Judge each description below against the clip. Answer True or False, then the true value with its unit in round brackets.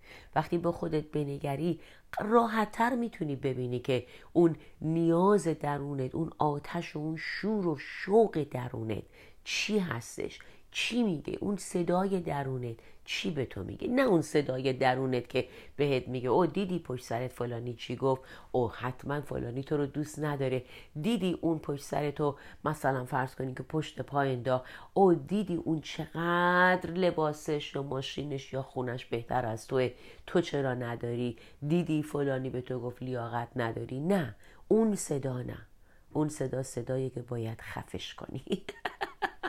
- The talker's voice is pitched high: False (140 Hz)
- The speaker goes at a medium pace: True (145 wpm)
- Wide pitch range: False (4.7 semitones)